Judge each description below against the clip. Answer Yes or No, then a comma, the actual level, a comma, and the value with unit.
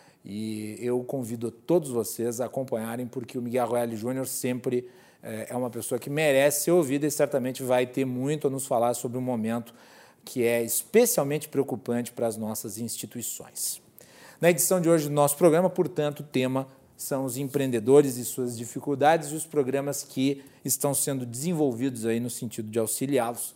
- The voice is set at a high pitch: No, low, 130 Hz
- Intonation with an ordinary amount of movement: Yes, average, 3.3 semitones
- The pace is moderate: Yes, average, 175 wpm